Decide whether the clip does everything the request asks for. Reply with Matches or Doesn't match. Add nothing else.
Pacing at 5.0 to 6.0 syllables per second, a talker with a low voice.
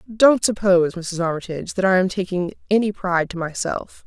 Doesn't match